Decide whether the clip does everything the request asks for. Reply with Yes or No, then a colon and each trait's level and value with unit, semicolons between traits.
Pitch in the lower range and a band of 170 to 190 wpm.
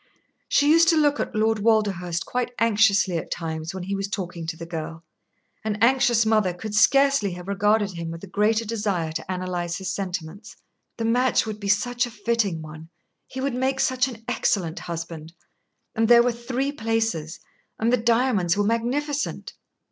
No: high, 210 Hz; average, 180 wpm